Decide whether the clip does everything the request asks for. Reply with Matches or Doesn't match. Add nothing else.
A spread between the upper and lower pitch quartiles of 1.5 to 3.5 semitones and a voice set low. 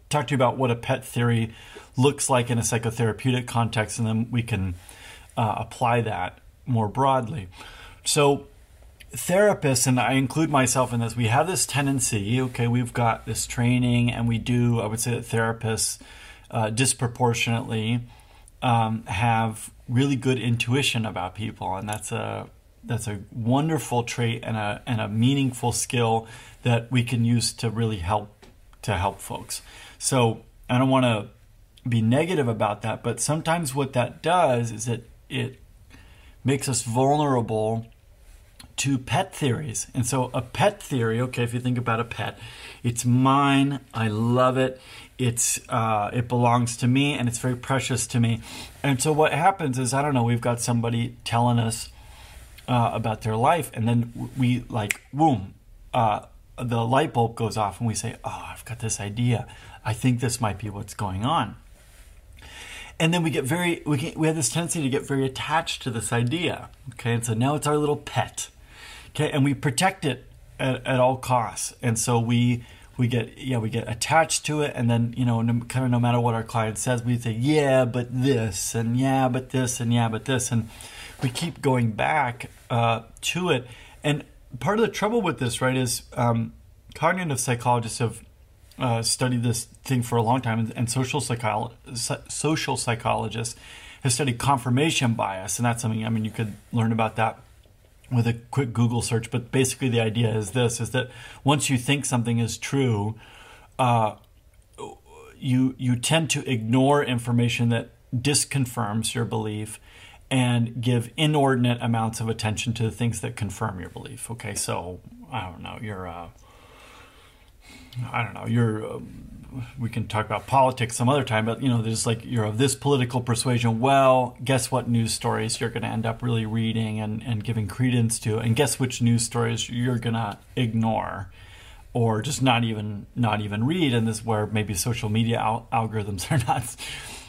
Matches